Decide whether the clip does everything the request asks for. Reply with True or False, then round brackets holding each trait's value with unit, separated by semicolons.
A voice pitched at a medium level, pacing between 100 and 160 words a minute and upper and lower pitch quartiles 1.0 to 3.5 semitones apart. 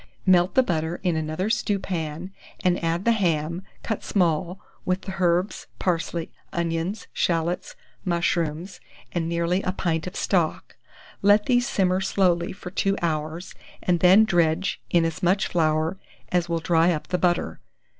True (175 Hz; 150 wpm; 2.4 semitones)